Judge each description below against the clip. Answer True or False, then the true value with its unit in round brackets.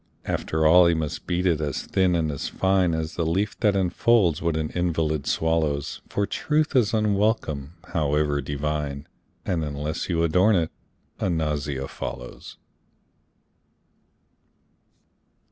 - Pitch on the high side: False (80 Hz)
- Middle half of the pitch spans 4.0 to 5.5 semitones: False (3.6 semitones)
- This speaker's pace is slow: True (130 wpm)